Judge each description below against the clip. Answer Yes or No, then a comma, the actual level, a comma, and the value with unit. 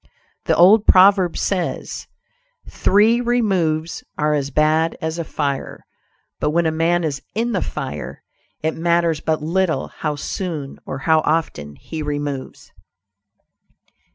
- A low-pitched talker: No, medium, 160 Hz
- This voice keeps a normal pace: No, slow, 130 wpm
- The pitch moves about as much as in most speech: Yes, average, 3.1 semitones